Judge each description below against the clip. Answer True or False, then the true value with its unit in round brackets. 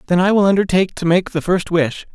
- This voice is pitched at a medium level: True (180 Hz)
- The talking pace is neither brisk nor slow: False (250 wpm)